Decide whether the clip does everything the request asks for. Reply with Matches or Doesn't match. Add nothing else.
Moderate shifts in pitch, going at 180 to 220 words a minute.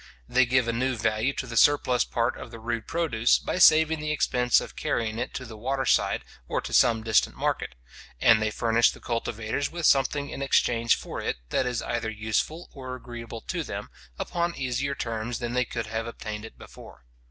Matches